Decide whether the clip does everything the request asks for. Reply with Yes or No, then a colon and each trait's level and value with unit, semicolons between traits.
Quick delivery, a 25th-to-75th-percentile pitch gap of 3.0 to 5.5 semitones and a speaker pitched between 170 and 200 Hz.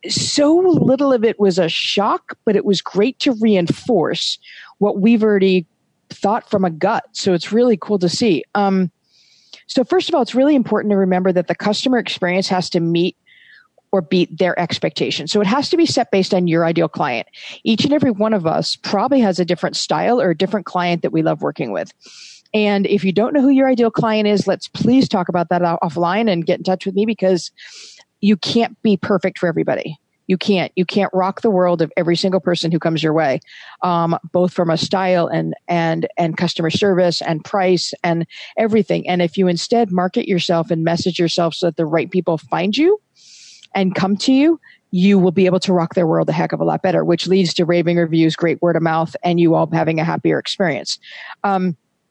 Yes: fast, 215 wpm; average, 3.7 semitones; medium, 185 Hz